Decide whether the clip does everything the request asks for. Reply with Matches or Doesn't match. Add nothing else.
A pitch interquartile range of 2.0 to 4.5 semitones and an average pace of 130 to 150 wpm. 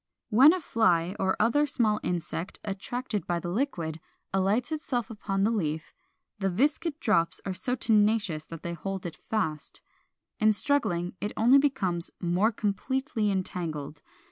Doesn't match